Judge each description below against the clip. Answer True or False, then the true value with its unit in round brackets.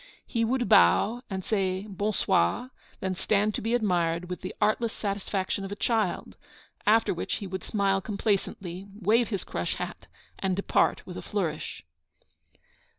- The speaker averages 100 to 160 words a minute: True (155 wpm)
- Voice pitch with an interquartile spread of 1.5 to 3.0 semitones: True (2.7 semitones)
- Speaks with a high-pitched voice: True (200 Hz)